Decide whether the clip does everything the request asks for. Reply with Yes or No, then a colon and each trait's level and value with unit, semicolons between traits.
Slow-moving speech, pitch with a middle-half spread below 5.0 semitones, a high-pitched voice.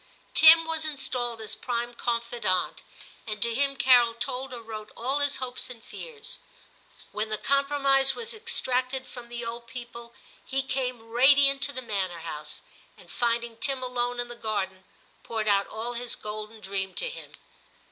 No: average, 165 wpm; average, 3.3 semitones; high, 240 Hz